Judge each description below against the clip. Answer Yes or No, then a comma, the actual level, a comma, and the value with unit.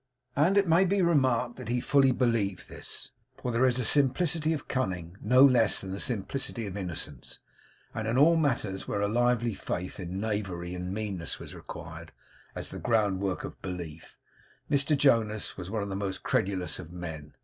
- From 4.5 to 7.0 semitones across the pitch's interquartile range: Yes, wide, 5.6 semitones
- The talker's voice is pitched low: Yes, low, 110 Hz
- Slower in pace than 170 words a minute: No, average, 185 wpm